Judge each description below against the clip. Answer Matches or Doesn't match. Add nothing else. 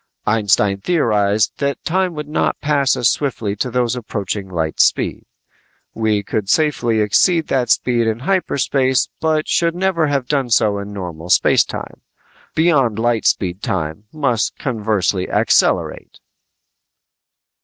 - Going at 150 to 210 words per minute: Doesn't match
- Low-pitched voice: Matches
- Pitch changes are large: Matches